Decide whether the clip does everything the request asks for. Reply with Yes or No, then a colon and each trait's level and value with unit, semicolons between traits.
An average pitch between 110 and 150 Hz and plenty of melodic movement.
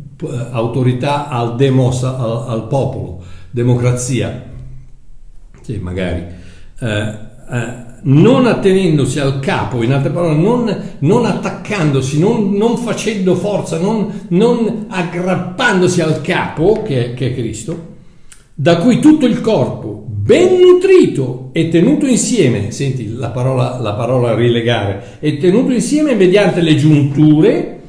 Yes: medium, 140 Hz; wide, 7.9 semitones